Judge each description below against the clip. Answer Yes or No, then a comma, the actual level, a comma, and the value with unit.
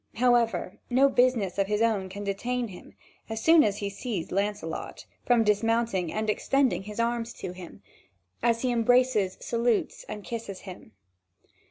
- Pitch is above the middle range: Yes, high, 225 Hz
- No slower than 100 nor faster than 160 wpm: Yes, average, 155 wpm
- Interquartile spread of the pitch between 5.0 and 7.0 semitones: No, average, 3.3 semitones